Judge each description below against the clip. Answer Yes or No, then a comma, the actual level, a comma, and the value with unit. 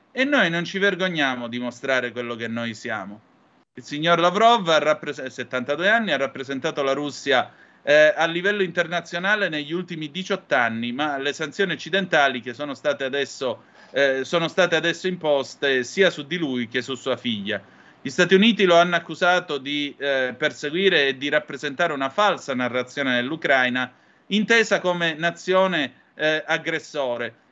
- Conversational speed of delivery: Yes, average, 155 wpm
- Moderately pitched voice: Yes, medium, 150 Hz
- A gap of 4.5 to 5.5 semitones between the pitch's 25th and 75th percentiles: Yes, average, 5.2 semitones